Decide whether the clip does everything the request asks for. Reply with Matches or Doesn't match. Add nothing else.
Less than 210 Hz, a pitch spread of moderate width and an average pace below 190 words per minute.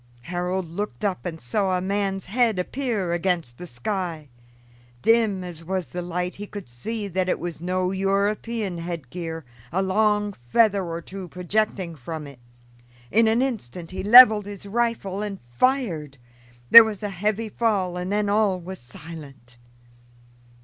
Matches